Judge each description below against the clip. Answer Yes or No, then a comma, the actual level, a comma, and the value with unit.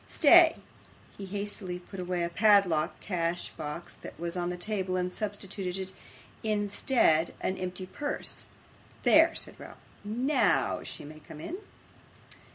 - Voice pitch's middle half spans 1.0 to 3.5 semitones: Yes, average, 2.9 semitones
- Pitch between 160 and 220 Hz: Yes, medium, 185 Hz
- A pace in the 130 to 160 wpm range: Yes, average, 145 wpm